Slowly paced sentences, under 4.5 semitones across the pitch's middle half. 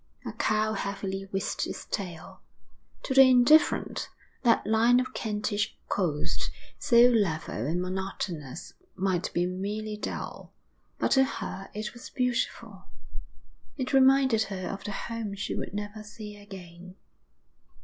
Yes: slow, 130 wpm; average, 3.7 semitones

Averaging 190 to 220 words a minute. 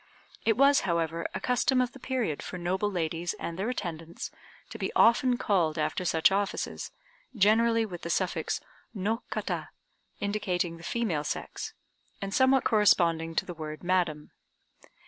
No: average, 150 wpm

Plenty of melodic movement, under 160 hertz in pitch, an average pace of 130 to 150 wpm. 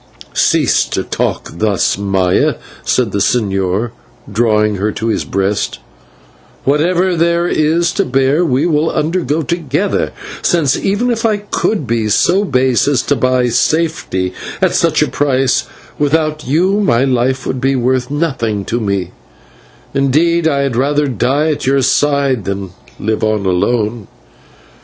Yes: wide, 6.4 semitones; low, 135 Hz; average, 145 wpm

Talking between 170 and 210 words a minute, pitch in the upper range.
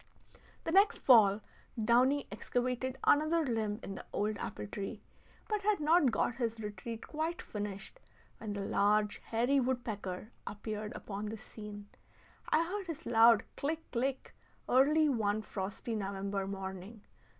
No: average, 140 wpm; high, 225 Hz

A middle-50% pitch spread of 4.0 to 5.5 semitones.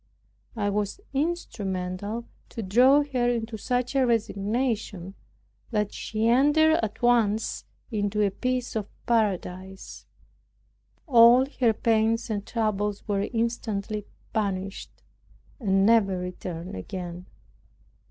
No: average, 3.3 semitones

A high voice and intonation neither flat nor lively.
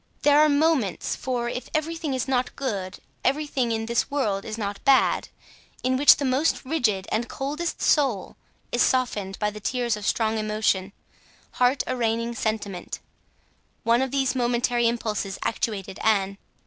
Yes: high, 240 Hz; average, 3.9 semitones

